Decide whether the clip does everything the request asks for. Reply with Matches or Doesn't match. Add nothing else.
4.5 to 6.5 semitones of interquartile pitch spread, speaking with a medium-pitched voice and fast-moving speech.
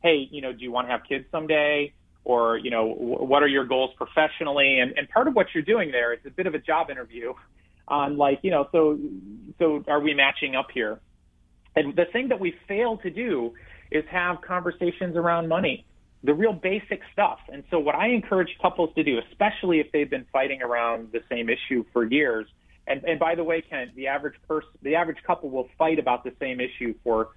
Matches